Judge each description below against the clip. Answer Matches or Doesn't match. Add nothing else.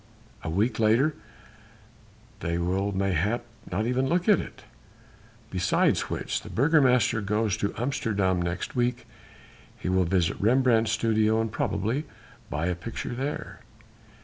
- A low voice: Matches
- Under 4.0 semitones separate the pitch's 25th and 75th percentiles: Doesn't match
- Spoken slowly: Matches